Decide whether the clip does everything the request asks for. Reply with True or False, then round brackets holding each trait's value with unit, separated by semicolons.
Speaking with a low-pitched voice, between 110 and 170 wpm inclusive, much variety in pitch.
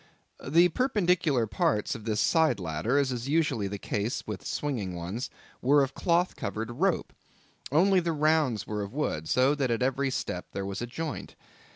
False (130 Hz; 180 wpm; 6.9 semitones)